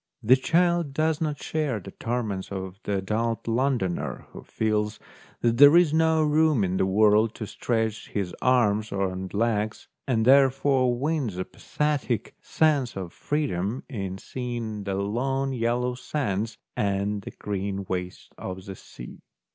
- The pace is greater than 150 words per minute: No, average, 145 wpm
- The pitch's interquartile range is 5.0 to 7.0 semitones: Yes, wide, 5.4 semitones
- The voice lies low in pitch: Yes, low, 115 Hz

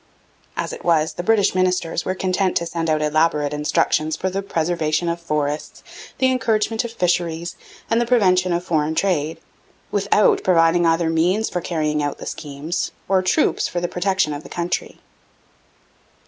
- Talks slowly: No, average, 165 wpm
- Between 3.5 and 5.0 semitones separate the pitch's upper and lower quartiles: No, average, 3.1 semitones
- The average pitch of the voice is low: No, medium, 170 Hz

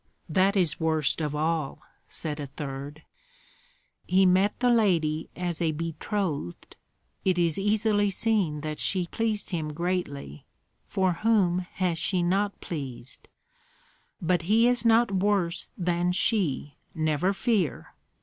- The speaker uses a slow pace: Yes, slow, 130 wpm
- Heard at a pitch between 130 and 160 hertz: No, medium, 175 Hz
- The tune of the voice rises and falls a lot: No, average, 4.3 semitones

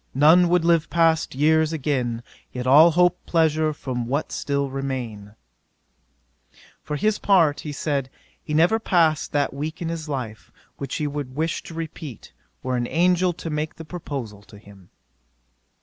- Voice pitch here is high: No, medium, 150 Hz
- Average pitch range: Yes, average, 3.8 semitones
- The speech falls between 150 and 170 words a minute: Yes, average, 160 wpm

